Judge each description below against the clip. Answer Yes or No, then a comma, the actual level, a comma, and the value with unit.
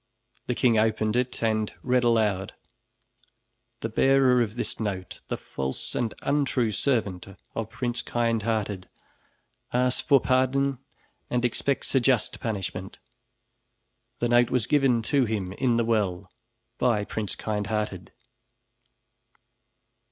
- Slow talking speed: Yes, slow, 120 wpm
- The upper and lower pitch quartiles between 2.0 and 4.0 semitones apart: Yes, average, 3.1 semitones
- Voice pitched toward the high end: No, low, 115 Hz